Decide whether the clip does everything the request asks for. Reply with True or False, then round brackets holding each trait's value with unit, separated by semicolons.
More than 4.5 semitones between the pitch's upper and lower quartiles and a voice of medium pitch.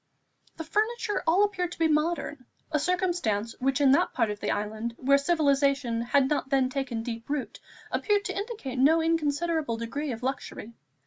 False (5.1 semitones; 280 Hz)